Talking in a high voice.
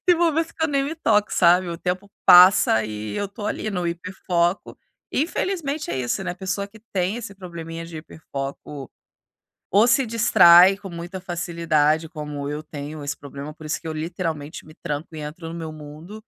No: medium, 170 Hz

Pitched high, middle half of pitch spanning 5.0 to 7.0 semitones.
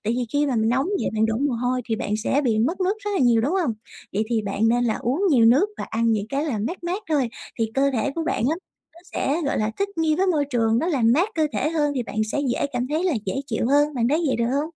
Yes: very high, 265 Hz; wide, 5.4 semitones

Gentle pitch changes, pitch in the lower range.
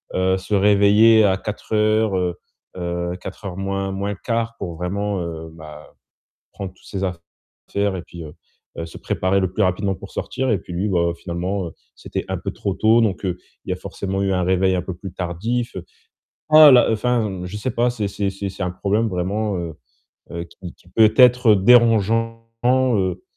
No: average, 3.2 semitones; very low, 95 Hz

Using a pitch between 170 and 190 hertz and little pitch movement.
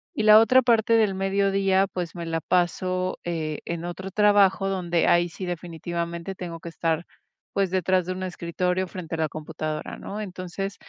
Yes: medium, 185 Hz; narrow, 2.3 semitones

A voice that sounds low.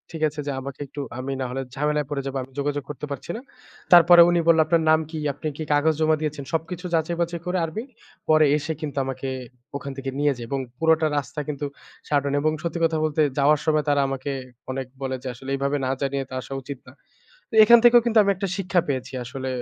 No: medium, 150 Hz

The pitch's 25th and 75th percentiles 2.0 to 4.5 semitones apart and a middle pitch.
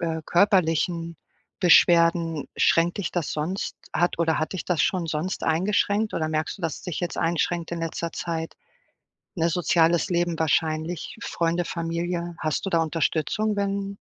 No: narrow, 1.6 semitones; medium, 170 Hz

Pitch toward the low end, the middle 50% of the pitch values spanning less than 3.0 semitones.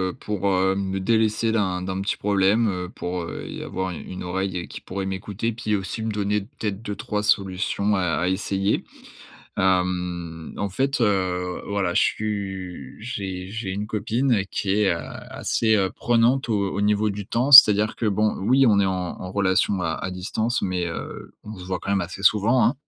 Yes: low, 100 Hz; narrow, 2.5 semitones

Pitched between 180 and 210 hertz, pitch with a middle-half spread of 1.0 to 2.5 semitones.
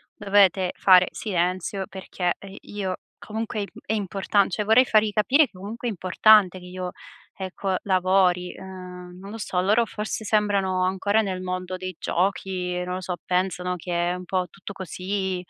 Yes: high, 190 Hz; narrow, 2.0 semitones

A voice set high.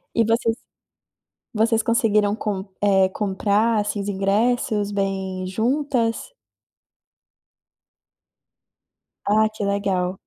Yes: high, 210 Hz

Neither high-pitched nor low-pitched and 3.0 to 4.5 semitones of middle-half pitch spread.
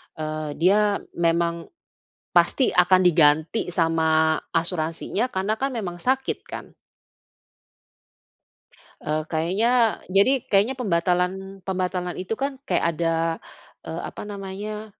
Yes: medium, 180 Hz; average, 4.0 semitones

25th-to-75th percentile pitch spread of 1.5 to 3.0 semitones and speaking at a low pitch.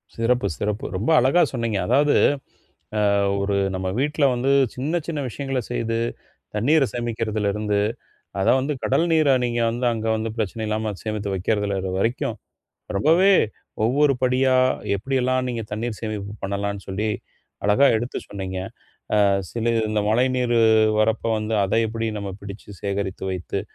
No: average, 3.8 semitones; low, 115 Hz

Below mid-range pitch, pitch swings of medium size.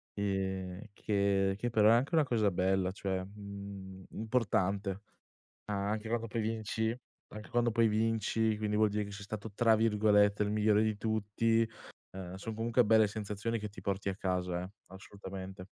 No: low, 105 Hz; narrow, 2.3 semitones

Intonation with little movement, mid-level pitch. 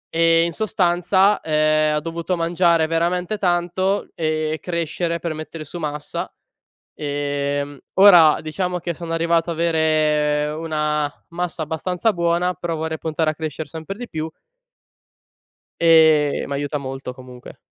Yes: narrow, 2.2 semitones; medium, 160 Hz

